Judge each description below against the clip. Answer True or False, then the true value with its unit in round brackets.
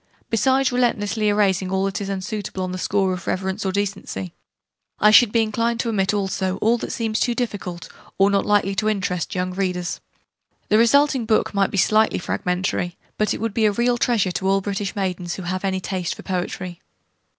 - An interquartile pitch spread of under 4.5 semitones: True (2.7 semitones)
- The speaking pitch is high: True (200 Hz)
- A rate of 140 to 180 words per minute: False (195 wpm)